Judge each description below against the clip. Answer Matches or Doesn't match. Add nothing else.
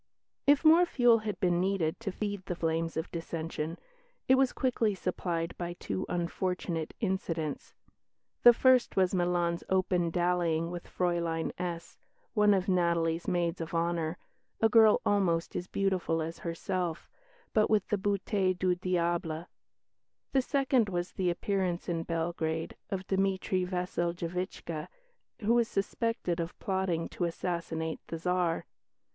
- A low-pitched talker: Doesn't match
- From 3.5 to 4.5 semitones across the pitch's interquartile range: Doesn't match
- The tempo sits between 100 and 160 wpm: Matches